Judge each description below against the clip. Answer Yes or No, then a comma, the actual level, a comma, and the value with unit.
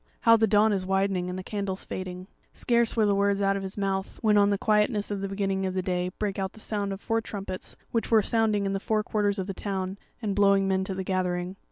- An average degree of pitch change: No, narrow, 1.6 semitones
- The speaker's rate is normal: No, fast, 250 wpm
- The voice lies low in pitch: No, high, 195 Hz